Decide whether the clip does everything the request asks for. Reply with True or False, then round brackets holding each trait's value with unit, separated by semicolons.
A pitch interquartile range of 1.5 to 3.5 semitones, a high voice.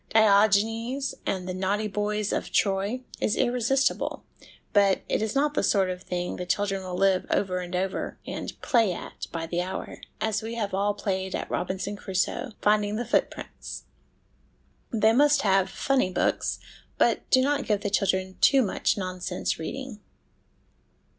True (3.1 semitones; 205 Hz)